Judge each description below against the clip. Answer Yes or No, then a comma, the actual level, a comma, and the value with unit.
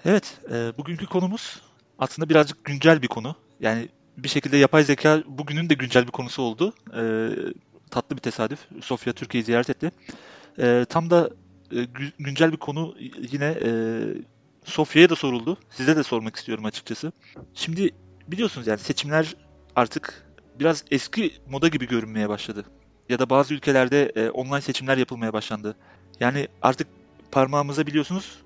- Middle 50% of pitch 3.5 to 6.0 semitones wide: Yes, average, 4.9 semitones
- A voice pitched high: No, low, 135 Hz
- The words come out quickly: Yes, fast, 150 wpm